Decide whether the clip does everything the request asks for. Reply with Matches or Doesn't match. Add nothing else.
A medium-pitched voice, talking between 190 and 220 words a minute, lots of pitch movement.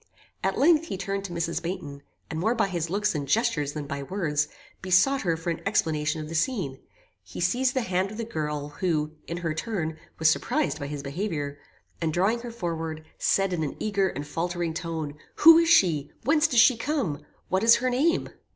Matches